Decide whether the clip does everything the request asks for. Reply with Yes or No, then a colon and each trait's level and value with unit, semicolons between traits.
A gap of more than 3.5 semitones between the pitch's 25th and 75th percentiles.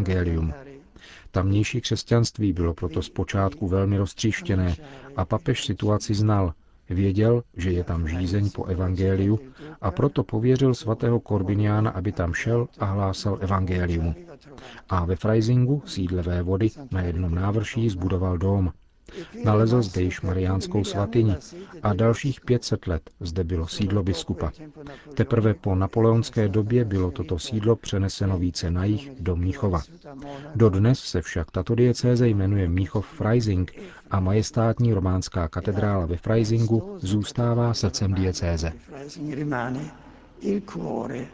Yes: average, 4.1 semitones